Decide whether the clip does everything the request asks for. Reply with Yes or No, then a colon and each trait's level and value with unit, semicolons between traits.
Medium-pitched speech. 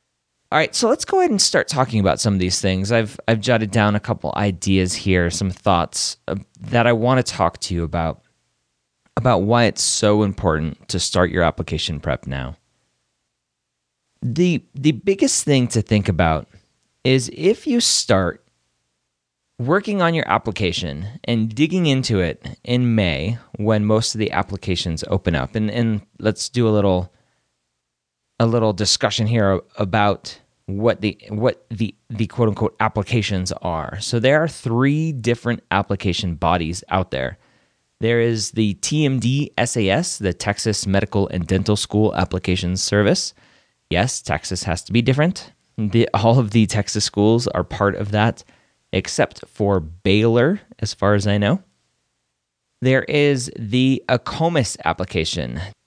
No: low, 105 Hz